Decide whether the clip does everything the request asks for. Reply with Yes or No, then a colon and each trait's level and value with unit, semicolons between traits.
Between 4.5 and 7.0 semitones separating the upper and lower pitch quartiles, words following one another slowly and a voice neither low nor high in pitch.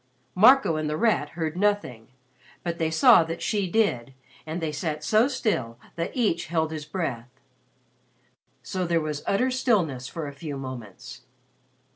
No: average, 5.3 semitones; average, 155 wpm; medium, 160 Hz